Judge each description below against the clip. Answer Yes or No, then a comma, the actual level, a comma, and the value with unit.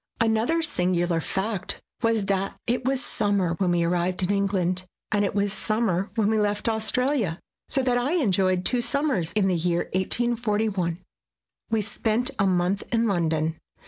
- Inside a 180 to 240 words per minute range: No, average, 160 wpm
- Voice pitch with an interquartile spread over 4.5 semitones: No, average, 4.0 semitones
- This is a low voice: No, high, 200 Hz